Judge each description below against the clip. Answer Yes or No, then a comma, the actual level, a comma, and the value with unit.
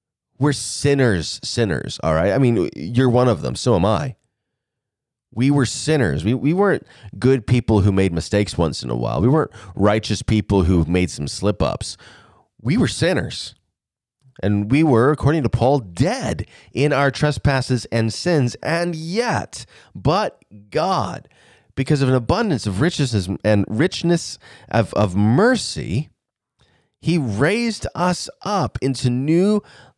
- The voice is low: Yes, low, 125 Hz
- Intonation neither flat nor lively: No, wide, 5.7 semitones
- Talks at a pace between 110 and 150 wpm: Yes, average, 145 wpm